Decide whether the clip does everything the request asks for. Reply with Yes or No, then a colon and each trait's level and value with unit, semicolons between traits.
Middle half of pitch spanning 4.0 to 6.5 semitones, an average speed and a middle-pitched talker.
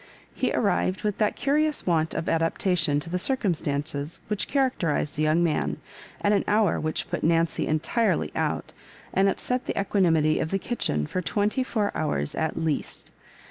Yes: average, 5.1 semitones; average, 170 wpm; medium, 170 Hz